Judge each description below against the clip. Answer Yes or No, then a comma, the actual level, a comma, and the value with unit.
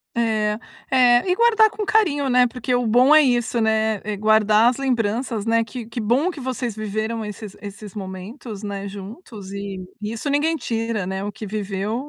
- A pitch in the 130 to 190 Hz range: No, high, 225 Hz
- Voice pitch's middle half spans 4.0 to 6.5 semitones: No, average, 3.2 semitones